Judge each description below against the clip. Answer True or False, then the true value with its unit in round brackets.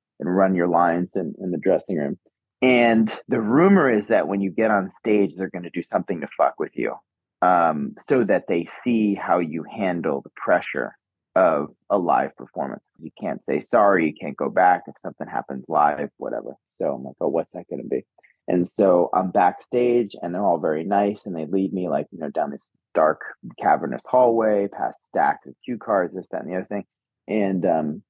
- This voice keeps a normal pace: False (210 wpm)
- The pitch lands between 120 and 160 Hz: False (95 Hz)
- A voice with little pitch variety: False (3.3 semitones)